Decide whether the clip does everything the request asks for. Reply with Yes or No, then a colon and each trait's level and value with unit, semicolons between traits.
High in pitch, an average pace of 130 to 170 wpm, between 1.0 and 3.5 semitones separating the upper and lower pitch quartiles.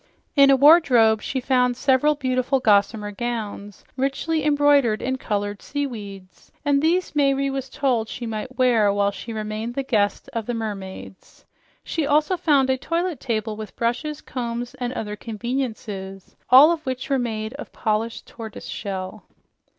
No: high, 245 Hz; average, 155 wpm; average, 4.3 semitones